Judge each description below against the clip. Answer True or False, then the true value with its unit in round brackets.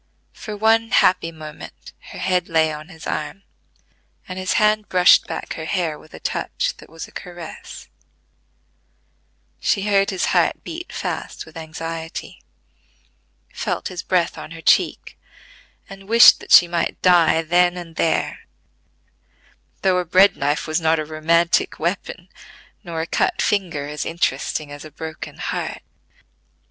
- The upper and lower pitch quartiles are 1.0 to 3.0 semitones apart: True (2.7 semitones)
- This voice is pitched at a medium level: True (170 Hz)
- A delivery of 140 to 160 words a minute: True (150 wpm)